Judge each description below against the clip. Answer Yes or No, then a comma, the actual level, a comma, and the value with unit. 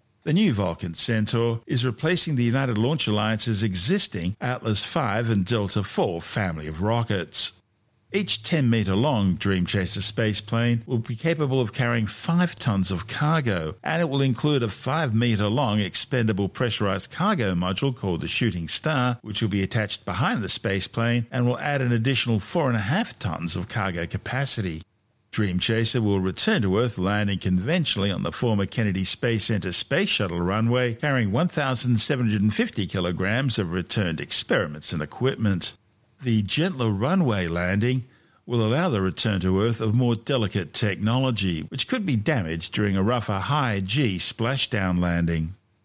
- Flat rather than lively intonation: No, average, 4.3 semitones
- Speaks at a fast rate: No, average, 155 wpm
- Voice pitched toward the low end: Yes, low, 110 Hz